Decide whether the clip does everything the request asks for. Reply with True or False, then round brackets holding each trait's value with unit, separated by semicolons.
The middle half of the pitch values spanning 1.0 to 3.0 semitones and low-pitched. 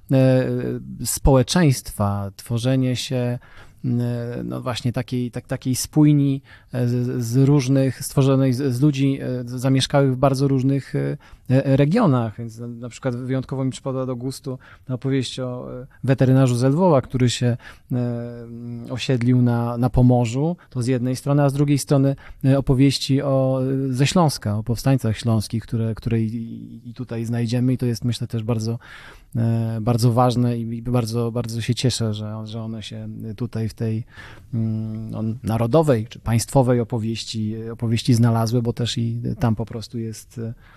True (2.5 semitones; 120 Hz)